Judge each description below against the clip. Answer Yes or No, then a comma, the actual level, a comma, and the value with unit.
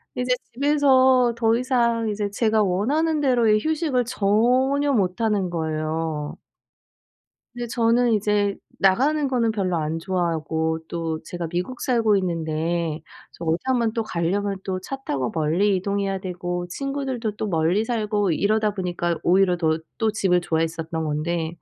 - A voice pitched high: Yes, high, 200 Hz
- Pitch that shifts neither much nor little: No, wide, 5.8 semitones